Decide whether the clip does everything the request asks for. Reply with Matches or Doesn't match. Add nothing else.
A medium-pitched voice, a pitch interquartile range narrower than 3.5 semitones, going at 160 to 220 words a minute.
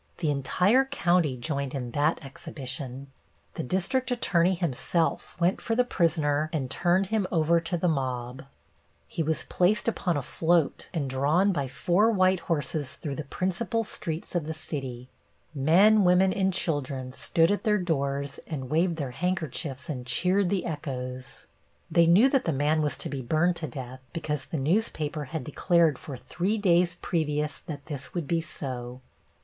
Doesn't match